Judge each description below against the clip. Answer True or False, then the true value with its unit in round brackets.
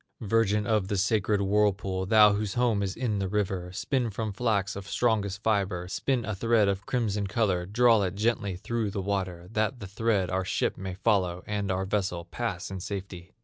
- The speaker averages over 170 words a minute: True (190 wpm)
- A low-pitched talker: True (100 Hz)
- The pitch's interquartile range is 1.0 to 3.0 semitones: True (2.4 semitones)